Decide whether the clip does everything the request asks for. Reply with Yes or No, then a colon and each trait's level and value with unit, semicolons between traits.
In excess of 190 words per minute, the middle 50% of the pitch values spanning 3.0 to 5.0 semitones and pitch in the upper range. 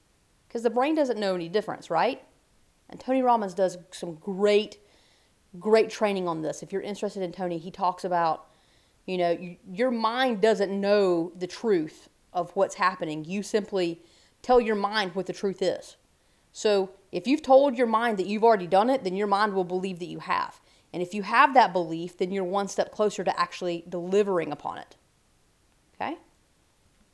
No: average, 185 wpm; average, 3.4 semitones; high, 195 Hz